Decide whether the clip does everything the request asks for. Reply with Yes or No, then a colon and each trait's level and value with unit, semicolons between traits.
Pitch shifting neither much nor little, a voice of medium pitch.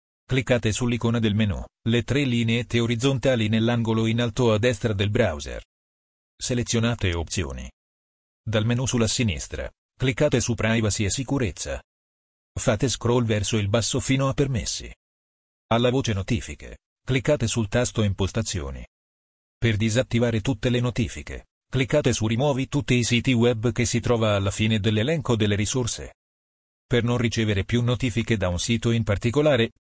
No: average, 4.4 semitones; low, 115 Hz